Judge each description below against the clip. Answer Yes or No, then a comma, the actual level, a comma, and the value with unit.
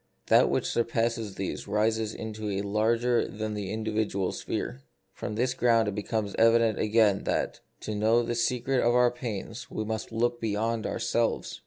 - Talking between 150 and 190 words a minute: Yes, average, 165 wpm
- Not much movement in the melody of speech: Yes, narrow, 1.8 semitones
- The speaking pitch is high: No, low, 110 Hz